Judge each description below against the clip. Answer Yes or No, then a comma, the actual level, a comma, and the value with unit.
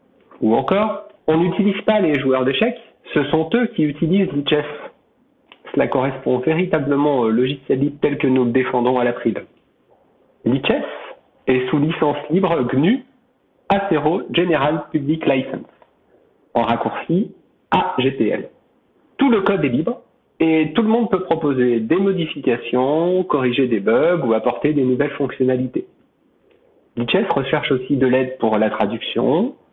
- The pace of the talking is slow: Yes, slow, 140 wpm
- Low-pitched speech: No, medium, 145 Hz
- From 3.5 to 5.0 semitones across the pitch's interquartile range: Yes, average, 4.4 semitones